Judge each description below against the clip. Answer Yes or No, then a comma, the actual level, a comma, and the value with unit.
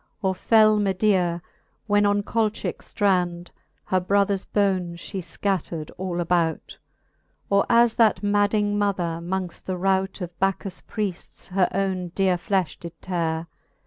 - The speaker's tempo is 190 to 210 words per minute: No, average, 140 wpm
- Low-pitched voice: No, high, 190 Hz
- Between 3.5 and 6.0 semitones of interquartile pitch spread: No, narrow, 2.6 semitones